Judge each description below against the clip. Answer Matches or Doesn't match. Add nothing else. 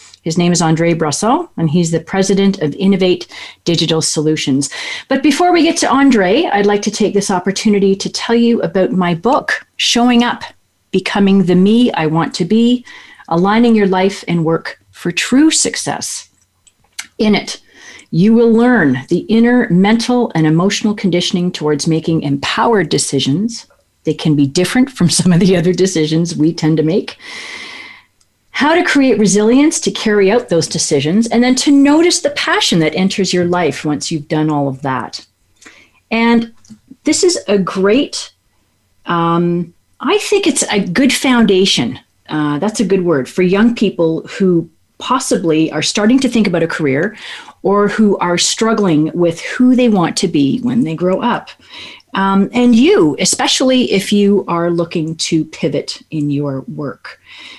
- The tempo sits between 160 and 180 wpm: Matches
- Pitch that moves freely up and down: Matches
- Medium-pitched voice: Doesn't match